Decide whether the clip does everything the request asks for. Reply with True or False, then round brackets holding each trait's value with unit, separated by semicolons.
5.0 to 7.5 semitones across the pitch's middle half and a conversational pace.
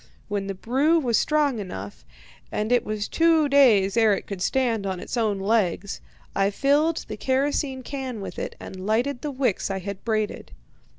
True (5.6 semitones; 180 wpm)